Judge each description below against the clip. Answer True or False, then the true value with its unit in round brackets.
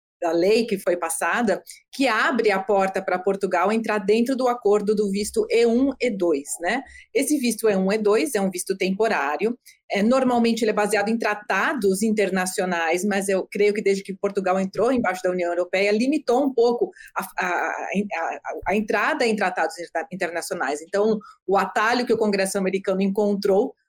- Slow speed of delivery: False (180 wpm)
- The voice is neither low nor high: False (205 Hz)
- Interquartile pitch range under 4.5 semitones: True (3.5 semitones)